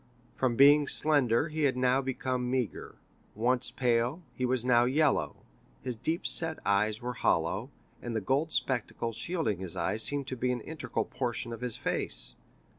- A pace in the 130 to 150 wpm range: No, average, 170 wpm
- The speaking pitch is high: No, low, 125 Hz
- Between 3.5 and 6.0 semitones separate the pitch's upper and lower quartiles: No, average, 3.1 semitones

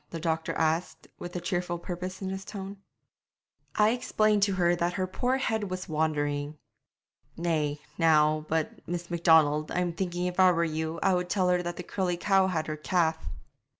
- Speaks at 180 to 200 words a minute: Yes, average, 185 wpm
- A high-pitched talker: No, medium, 175 Hz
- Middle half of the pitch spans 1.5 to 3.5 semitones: Yes, narrow, 2.6 semitones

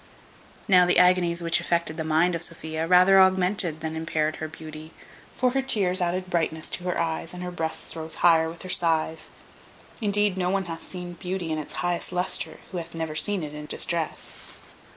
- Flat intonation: Yes, narrow, 2.2 semitones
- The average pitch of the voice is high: No, medium, 170 Hz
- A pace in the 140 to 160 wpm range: No, average, 195 wpm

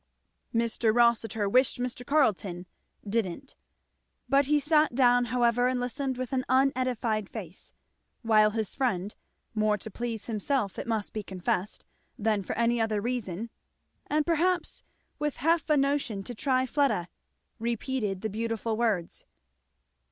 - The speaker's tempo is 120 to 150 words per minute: Yes, slow, 135 wpm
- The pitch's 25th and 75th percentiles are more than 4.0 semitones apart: No, average, 3.5 semitones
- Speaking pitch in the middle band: No, high, 235 Hz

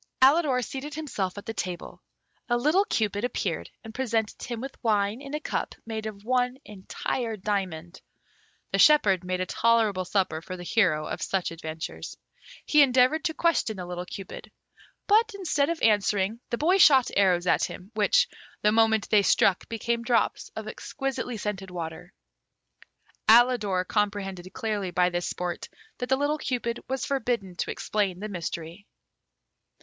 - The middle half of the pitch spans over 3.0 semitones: Yes, average, 5.2 semitones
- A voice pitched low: No, high, 215 Hz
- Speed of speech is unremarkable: Yes, average, 160 wpm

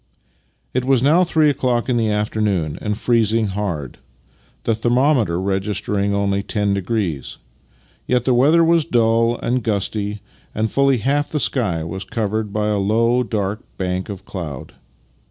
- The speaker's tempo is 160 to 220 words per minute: No, average, 150 wpm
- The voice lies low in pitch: Yes, low, 110 Hz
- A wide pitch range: No, average, 3.8 semitones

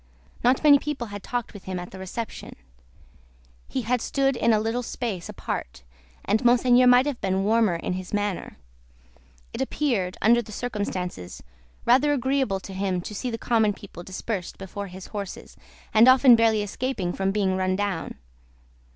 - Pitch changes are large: No, average, 4.5 semitones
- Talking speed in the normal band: Yes, average, 170 wpm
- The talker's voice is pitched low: No, high, 215 Hz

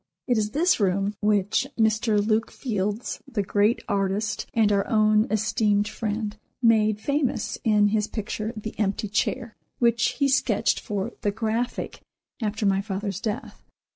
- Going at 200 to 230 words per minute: No, average, 145 wpm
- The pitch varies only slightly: Yes, narrow, 1.7 semitones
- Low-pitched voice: No, high, 215 Hz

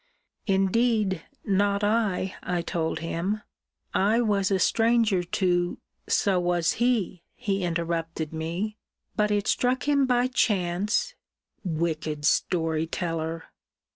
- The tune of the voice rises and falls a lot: No, average, 4.1 semitones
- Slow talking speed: Yes, slow, 110 wpm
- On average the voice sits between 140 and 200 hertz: Yes, high, 190 Hz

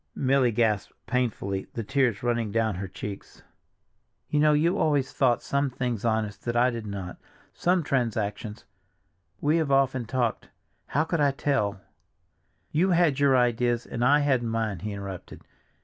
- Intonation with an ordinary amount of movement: Yes, average, 4.9 semitones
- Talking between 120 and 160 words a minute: Yes, average, 150 wpm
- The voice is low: Yes, low, 120 Hz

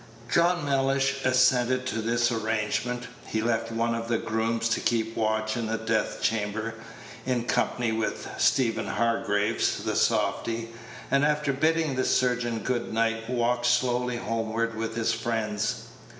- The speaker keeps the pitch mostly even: Yes, narrow, 1.9 semitones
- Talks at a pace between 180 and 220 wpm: No, average, 145 wpm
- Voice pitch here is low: Yes, low, 115 Hz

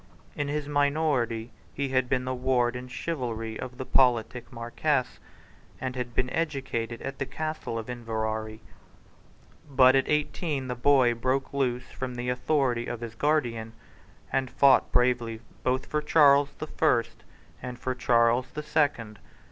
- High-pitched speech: No, low, 125 Hz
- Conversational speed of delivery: Yes, average, 150 wpm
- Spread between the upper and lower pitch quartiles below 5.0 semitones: Yes, average, 2.9 semitones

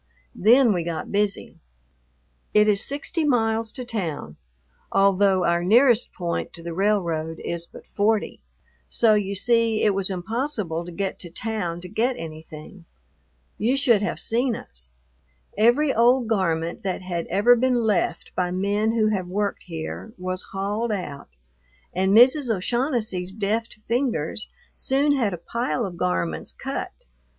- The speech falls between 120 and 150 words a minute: Yes, average, 145 wpm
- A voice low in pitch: No, high, 205 Hz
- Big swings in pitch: No, average, 4.7 semitones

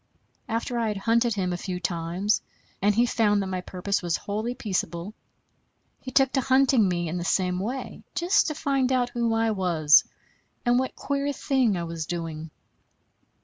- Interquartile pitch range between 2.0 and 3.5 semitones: No, wide, 5.5 semitones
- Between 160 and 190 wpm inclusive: Yes, average, 180 wpm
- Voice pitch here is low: No, high, 210 Hz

